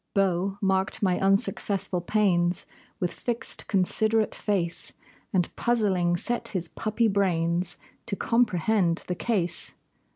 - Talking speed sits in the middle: No, slow, 110 wpm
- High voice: Yes, high, 195 Hz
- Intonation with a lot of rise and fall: No, average, 3.4 semitones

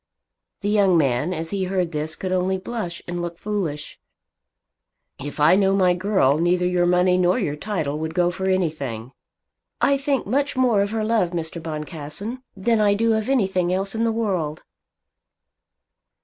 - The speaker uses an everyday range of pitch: Yes, average, 4.2 semitones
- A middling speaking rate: Yes, average, 170 wpm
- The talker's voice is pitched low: No, medium, 185 Hz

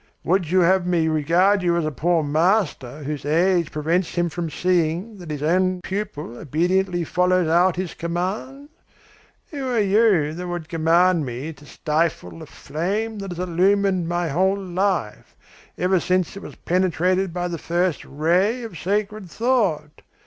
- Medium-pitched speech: Yes, medium, 175 Hz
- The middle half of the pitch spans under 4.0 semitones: Yes, average, 3.0 semitones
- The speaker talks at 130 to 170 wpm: Yes, average, 160 wpm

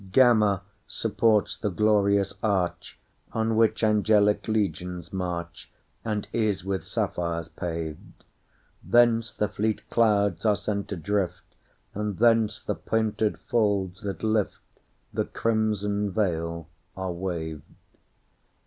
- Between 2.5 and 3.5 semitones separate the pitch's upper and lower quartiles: Yes, average, 2.9 semitones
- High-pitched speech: No, low, 100 Hz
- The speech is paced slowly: Yes, slow, 95 wpm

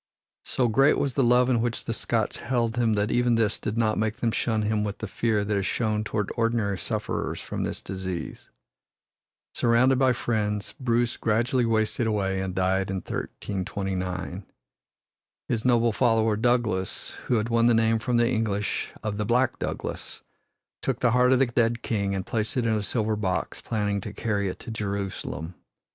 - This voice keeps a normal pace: Yes, average, 185 wpm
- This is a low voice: Yes, low, 110 Hz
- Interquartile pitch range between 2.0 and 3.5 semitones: Yes, narrow, 2.6 semitones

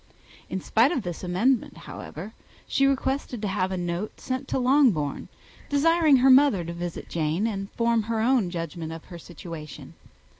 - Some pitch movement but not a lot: No, wide, 7.1 semitones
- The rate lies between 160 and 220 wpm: Yes, average, 165 wpm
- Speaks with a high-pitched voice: Yes, high, 210 Hz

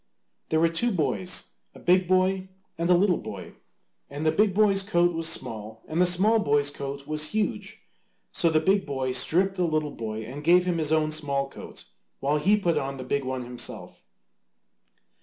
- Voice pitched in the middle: Yes, medium, 155 Hz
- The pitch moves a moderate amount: Yes, average, 4.8 semitones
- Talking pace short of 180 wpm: No, average, 190 wpm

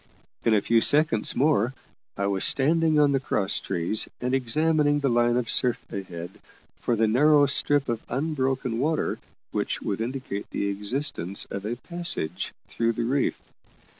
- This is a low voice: Yes, low, 125 Hz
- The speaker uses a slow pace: No, average, 160 wpm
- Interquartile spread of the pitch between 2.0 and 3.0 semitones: No, average, 5.1 semitones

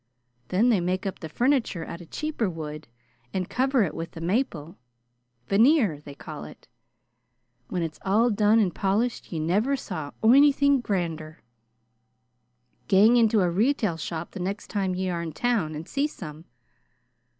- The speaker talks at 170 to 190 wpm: No, average, 160 wpm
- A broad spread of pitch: Yes, wide, 6.1 semitones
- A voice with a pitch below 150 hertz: No, high, 190 Hz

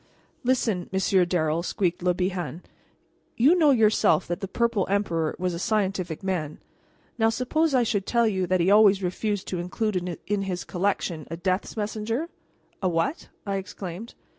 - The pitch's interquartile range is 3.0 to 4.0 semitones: Yes, average, 3.5 semitones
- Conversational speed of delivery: Yes, average, 165 wpm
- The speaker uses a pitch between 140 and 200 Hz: Yes, high, 190 Hz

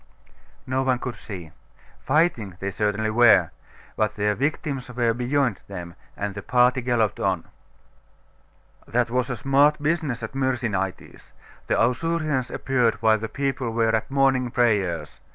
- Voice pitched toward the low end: Yes, low, 120 Hz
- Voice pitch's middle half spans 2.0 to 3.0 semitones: No, average, 3.9 semitones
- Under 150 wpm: Yes, average, 140 wpm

